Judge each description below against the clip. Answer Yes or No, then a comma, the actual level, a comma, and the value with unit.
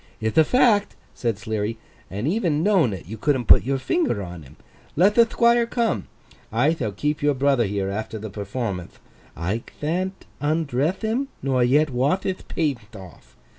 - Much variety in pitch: Yes, wide, 8.5 semitones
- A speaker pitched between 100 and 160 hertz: Yes, low, 135 Hz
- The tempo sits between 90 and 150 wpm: No, average, 170 wpm